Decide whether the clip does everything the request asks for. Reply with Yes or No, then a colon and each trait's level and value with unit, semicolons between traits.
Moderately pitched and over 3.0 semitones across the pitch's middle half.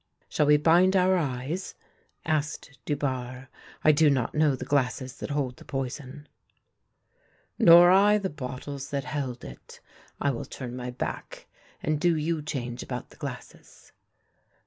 Yes: medium, 145 Hz; average, 3.4 semitones